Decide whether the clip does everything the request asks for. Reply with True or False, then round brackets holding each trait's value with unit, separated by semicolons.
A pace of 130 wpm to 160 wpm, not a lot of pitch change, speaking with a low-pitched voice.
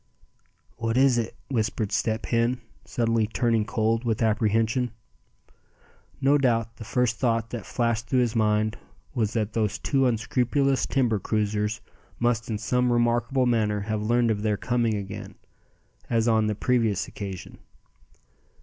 True (140 wpm; 2.0 semitones; 115 Hz)